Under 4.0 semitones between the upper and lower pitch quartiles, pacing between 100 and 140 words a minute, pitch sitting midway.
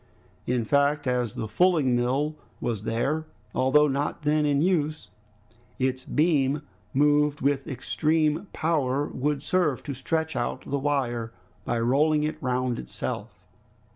Yes: average, 3.0 semitones; slow, 135 wpm; medium, 145 Hz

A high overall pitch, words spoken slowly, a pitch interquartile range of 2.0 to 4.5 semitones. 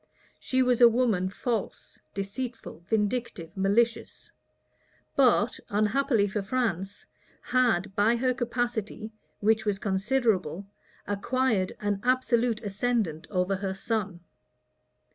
Yes: high, 220 Hz; slow, 105 wpm; average, 3.8 semitones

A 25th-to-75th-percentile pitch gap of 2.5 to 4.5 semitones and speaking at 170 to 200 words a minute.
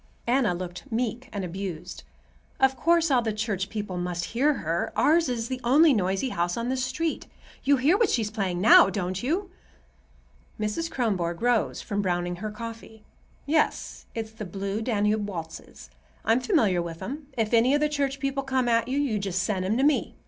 No: wide, 5.5 semitones; average, 185 wpm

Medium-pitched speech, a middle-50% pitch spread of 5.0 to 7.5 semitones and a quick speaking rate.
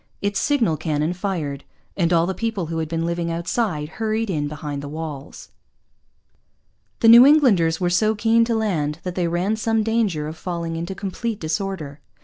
No: medium, 175 Hz; wide, 5.4 semitones; average, 175 wpm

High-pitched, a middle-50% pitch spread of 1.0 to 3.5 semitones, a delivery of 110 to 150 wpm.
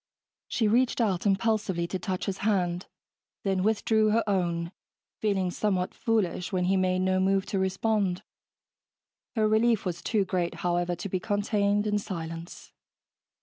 Yes: high, 195 Hz; average, 2.7 semitones; average, 145 wpm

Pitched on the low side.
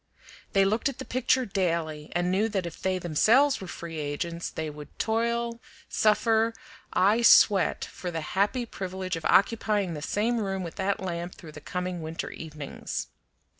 No: high, 190 Hz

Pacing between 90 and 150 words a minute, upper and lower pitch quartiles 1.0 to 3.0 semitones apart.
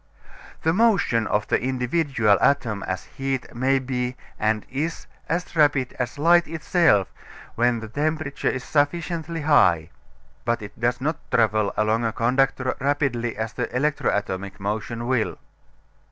No: average, 140 wpm; average, 4.8 semitones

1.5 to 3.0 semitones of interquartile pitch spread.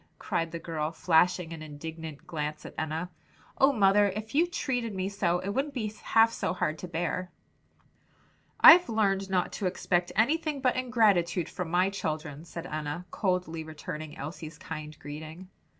No: average, 4.9 semitones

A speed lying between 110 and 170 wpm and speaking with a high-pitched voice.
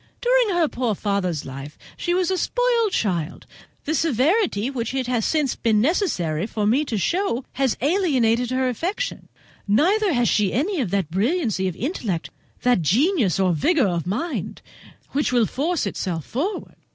Yes: average, 165 wpm; very high, 250 Hz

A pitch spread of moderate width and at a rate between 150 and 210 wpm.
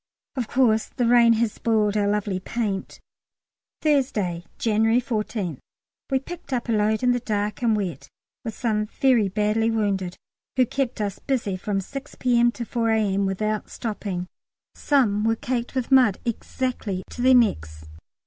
Yes: average, 3.1 semitones; average, 160 wpm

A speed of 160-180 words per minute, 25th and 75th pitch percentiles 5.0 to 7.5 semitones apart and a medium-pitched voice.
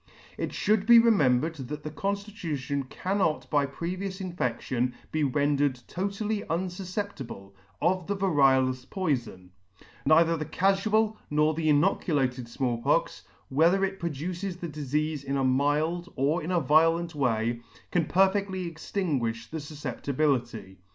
No: slow, 135 wpm; wide, 5.4 semitones; medium, 155 Hz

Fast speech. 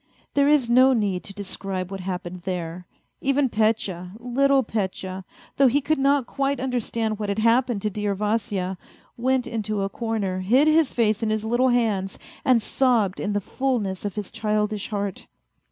No: average, 175 wpm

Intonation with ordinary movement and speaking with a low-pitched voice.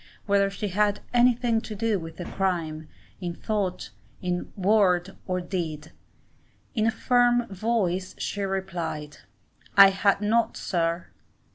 No: average, 3.5 semitones; high, 195 Hz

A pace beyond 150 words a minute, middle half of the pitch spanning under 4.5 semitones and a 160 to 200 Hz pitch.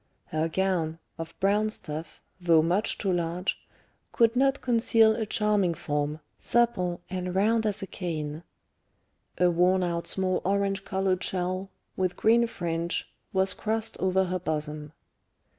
No: average, 140 wpm; average, 3.6 semitones; medium, 185 Hz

